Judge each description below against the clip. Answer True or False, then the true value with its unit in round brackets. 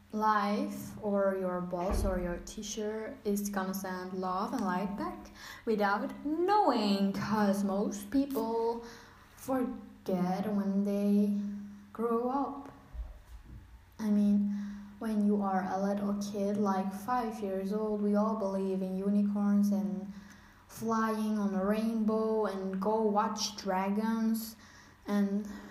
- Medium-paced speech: False (120 wpm)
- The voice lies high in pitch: True (205 Hz)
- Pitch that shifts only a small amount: True (2.0 semitones)